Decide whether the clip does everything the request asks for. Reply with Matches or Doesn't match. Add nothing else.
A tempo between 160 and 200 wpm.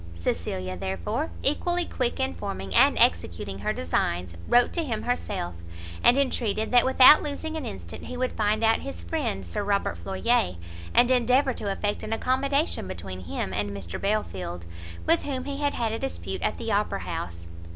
Matches